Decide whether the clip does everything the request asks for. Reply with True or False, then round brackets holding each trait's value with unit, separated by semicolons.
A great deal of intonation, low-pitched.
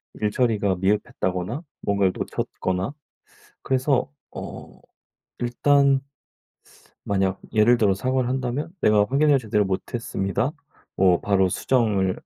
False (5.0 semitones; 105 Hz)